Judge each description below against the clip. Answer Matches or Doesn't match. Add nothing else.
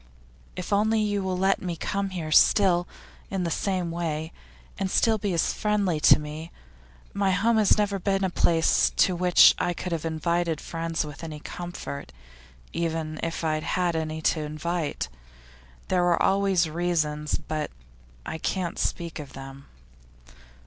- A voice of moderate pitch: Matches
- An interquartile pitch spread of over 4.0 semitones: Doesn't match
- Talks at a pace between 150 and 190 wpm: Matches